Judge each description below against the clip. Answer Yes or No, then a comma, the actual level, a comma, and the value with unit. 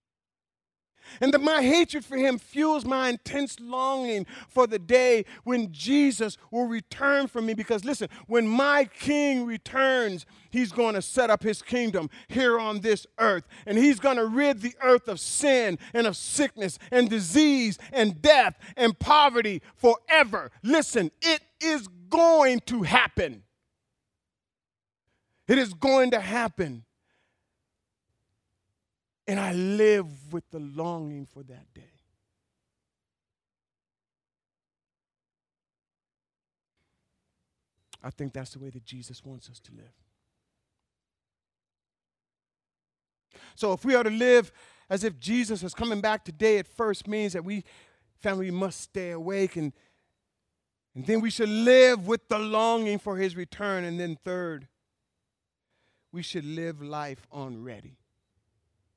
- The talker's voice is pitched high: Yes, high, 210 Hz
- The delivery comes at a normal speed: No, slow, 130 wpm